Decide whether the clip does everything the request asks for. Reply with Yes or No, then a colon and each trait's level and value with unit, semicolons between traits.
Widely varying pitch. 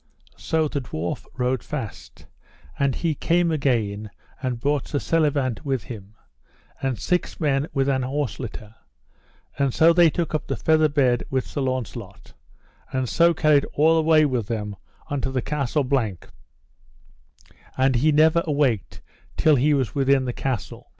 No: average, 3.5 semitones